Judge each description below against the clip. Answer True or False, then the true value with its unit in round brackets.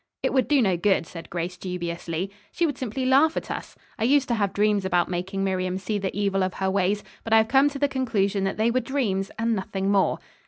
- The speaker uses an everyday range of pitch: True (4.2 semitones)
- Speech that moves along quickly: True (240 wpm)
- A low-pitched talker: False (200 Hz)